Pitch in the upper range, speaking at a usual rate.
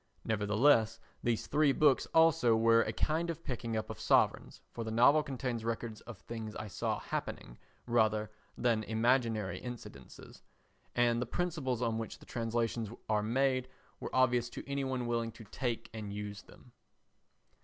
No: low, 115 Hz; average, 160 wpm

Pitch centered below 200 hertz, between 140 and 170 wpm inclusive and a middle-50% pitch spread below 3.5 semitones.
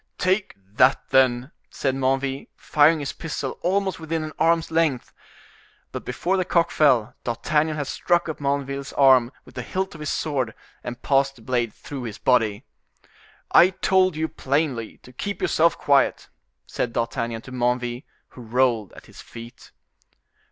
No: low, 135 Hz; average, 160 wpm; average, 4.5 semitones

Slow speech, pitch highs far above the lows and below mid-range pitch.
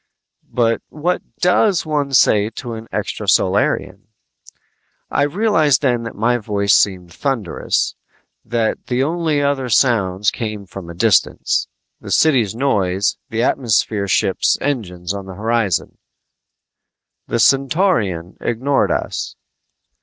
Yes: slow, 115 wpm; wide, 5.7 semitones; low, 115 Hz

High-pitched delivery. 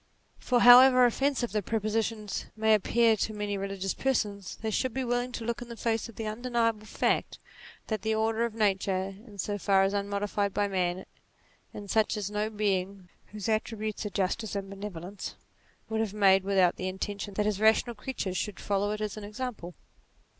Yes: high, 210 Hz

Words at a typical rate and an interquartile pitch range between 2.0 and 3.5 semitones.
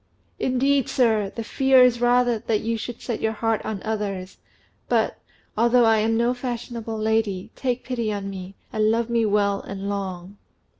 Yes: average, 170 wpm; average, 2.8 semitones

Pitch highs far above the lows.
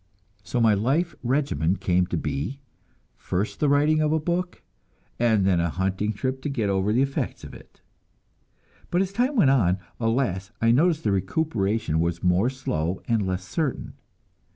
Yes: wide, 7.2 semitones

